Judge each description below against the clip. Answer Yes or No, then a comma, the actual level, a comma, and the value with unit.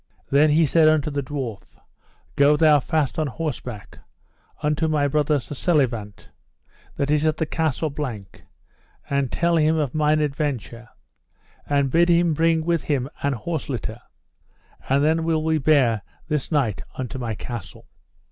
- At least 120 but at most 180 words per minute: Yes, average, 155 wpm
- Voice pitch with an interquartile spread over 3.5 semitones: No, average, 3.2 semitones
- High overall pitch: No, medium, 150 Hz